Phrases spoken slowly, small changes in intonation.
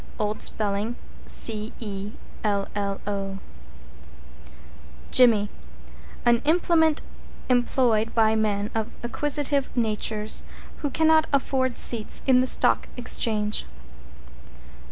No: slow, 80 wpm; average, 3.6 semitones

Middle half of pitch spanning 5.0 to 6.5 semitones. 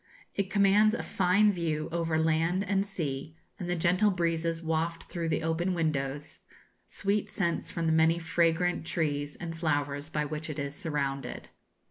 No: average, 2.7 semitones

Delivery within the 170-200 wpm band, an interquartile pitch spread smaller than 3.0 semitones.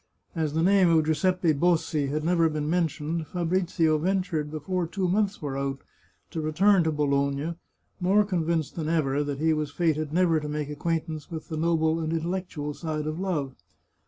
Yes: average, 180 wpm; narrow, 2.6 semitones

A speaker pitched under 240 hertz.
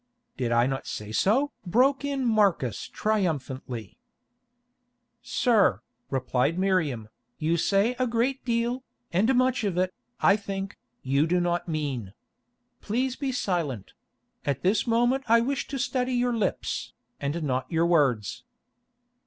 Yes: high, 190 Hz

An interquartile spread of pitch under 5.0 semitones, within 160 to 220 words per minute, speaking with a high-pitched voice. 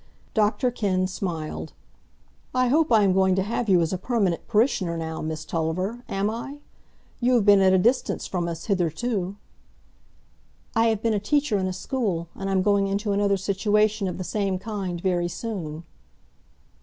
Yes: average, 3.3 semitones; average, 170 wpm; high, 195 Hz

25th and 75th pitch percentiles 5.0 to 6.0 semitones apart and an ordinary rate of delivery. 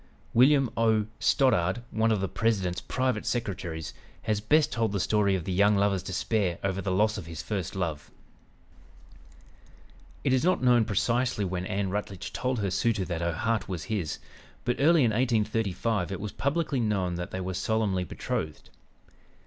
No: average, 3.8 semitones; average, 170 wpm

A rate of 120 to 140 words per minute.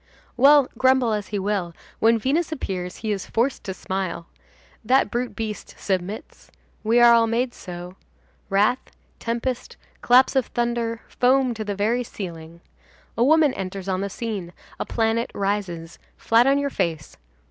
No: average, 155 wpm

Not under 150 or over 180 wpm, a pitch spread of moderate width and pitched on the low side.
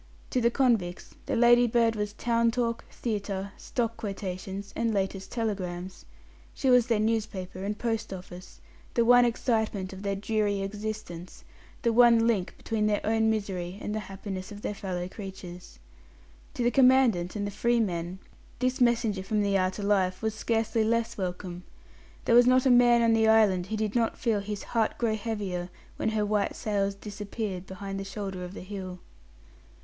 No: average, 175 wpm; average, 3.1 semitones; high, 210 Hz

